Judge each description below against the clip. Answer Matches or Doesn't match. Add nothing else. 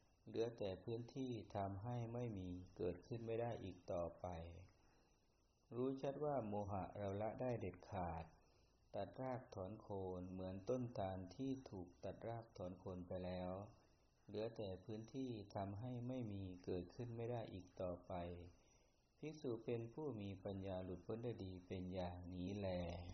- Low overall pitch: Matches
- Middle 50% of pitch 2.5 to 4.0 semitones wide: Doesn't match